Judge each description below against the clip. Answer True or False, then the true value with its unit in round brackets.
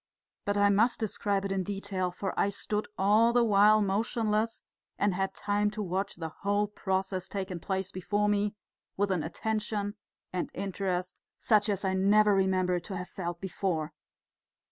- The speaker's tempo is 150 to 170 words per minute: True (165 wpm)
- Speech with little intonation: True (1.7 semitones)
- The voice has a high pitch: True (200 Hz)